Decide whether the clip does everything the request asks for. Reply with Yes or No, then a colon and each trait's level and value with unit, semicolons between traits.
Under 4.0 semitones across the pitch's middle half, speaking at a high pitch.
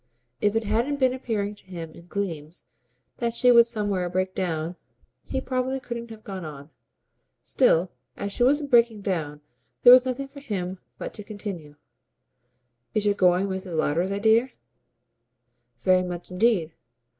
No: average, 4.8 semitones; high, 200 Hz